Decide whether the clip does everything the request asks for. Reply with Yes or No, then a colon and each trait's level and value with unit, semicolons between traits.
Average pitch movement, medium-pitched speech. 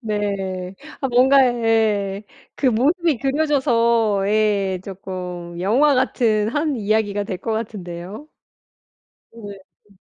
No: average, 4.3 semitones; high, 215 Hz